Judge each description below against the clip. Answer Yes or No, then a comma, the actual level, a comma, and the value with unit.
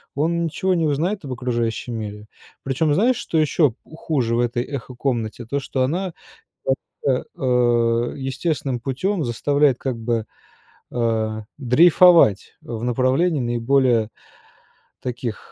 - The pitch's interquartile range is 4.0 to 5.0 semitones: Yes, average, 4.7 semitones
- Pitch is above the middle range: No, low, 130 Hz